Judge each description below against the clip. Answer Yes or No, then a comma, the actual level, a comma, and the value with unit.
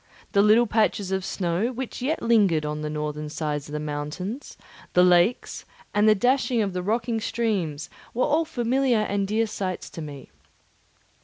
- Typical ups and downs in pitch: No, wide, 6.7 semitones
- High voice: Yes, high, 200 Hz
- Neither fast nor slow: Yes, average, 170 wpm